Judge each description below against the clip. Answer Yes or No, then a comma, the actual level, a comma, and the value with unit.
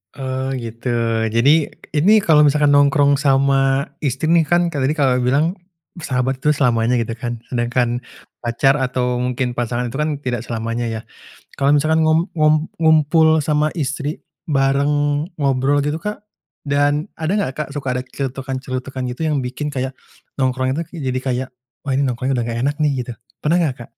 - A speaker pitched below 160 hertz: Yes, low, 135 Hz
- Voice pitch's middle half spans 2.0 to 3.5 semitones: Yes, average, 3.0 semitones